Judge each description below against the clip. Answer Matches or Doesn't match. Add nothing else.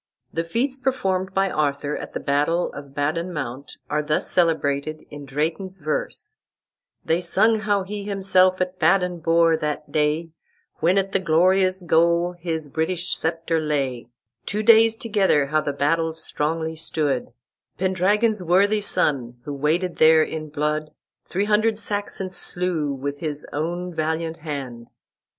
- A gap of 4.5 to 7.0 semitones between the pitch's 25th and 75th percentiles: Doesn't match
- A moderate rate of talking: Matches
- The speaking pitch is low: Doesn't match